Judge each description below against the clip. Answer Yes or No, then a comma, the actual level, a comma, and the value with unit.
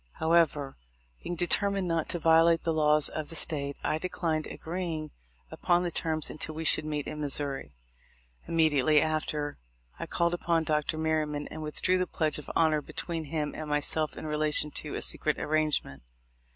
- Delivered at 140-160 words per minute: No, average, 175 wpm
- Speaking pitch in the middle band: Yes, medium, 155 Hz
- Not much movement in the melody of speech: Yes, narrow, 1.6 semitones